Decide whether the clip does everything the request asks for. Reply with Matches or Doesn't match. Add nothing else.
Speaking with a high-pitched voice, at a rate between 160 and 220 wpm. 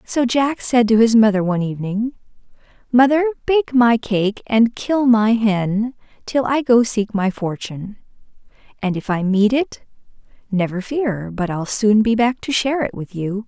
Matches